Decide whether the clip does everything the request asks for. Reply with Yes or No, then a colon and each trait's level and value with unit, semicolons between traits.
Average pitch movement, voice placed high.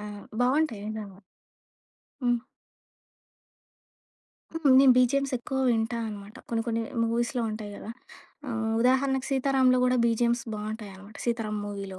Yes: average, 3.0 semitones; high, 235 Hz